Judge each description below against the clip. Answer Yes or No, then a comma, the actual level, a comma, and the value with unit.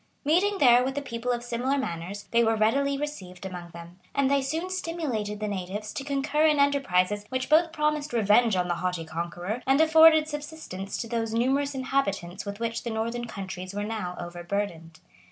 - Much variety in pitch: Yes, wide, 6.7 semitones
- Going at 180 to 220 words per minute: Yes, average, 185 wpm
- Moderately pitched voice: No, high, 230 Hz